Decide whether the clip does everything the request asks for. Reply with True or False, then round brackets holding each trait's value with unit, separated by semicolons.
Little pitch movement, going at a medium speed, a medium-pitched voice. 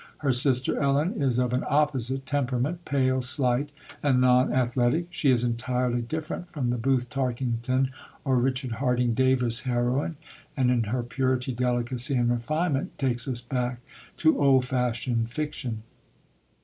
False (2.0 semitones; 145 wpm; 125 Hz)